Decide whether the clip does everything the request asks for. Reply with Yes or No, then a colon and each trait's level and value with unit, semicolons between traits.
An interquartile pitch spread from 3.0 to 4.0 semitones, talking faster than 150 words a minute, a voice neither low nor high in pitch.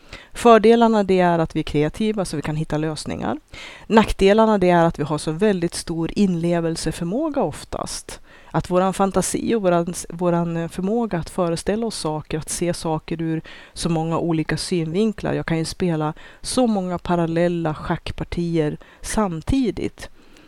No: average, 3.4 semitones; average, 145 wpm; medium, 170 Hz